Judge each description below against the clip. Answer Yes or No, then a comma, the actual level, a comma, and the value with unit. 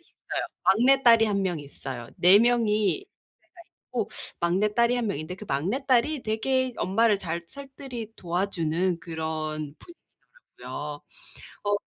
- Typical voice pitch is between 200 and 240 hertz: Yes, high, 205 Hz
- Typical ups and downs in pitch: No, wide, 6.4 semitones